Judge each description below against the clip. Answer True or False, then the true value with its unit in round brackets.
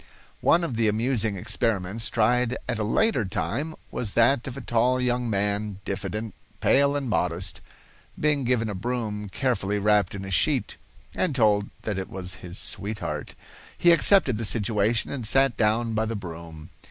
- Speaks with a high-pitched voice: False (110 Hz)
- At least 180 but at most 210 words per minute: False (165 wpm)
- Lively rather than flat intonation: False (3.7 semitones)